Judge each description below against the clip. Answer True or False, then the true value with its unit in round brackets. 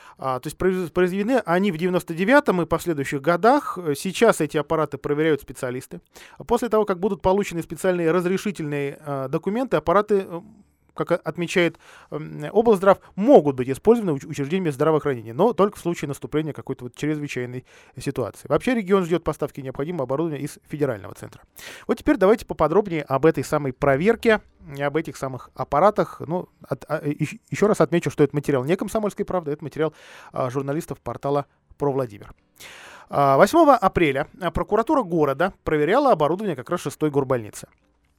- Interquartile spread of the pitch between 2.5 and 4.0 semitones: False (5.1 semitones)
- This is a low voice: False (160 Hz)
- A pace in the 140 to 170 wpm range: True (150 wpm)